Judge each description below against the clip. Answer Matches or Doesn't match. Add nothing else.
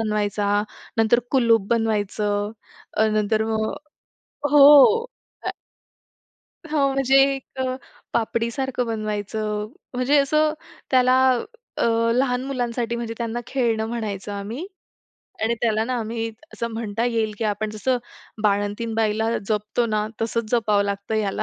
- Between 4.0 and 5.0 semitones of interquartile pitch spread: Doesn't match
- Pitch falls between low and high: Doesn't match